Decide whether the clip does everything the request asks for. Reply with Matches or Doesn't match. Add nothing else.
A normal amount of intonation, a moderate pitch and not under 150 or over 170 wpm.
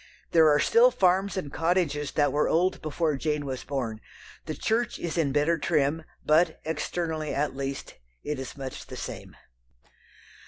Matches